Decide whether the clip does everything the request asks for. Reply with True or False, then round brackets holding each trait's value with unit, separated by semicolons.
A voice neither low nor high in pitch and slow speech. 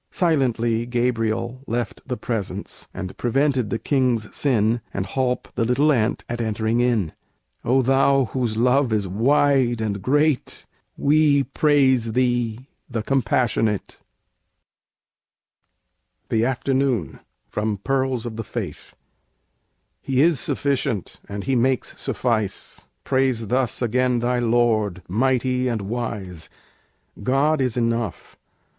False (120 Hz; 115 wpm)